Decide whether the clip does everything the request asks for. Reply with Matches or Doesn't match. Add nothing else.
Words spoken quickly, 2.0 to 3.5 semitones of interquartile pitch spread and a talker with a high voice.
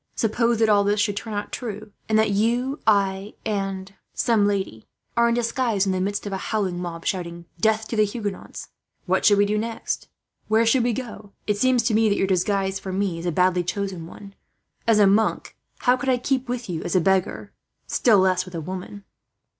Matches